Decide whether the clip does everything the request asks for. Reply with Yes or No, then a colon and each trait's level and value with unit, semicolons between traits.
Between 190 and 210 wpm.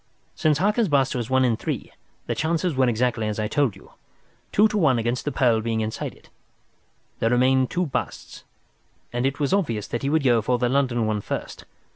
Yes: average, 200 wpm